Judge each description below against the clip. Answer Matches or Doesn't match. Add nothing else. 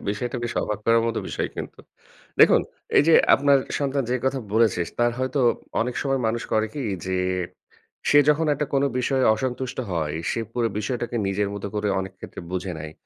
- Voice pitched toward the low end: Matches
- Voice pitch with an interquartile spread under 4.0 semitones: Doesn't match